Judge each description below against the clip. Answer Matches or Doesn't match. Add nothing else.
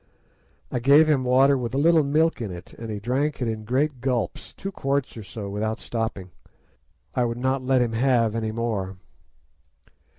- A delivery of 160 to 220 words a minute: Matches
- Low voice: Matches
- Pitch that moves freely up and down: Doesn't match